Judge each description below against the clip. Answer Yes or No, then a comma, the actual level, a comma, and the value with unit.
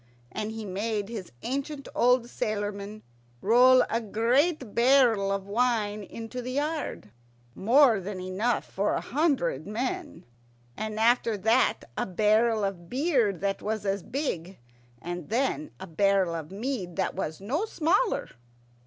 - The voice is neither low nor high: No, high, 220 Hz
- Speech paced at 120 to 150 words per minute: Yes, average, 140 wpm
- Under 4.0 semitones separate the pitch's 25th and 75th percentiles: No, average, 4.4 semitones